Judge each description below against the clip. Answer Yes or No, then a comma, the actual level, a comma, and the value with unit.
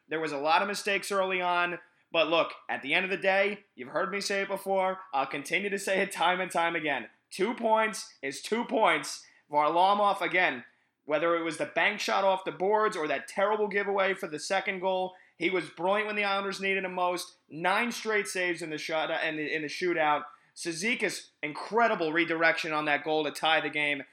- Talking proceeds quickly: Yes, fast, 215 wpm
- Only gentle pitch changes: No, average, 3.8 semitones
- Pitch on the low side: No, medium, 180 Hz